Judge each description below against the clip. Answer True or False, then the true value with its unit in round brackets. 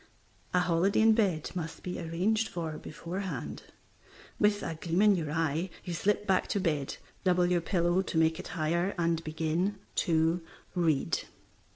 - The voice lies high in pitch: False (175 Hz)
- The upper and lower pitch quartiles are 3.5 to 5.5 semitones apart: False (2.8 semitones)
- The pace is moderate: True (160 wpm)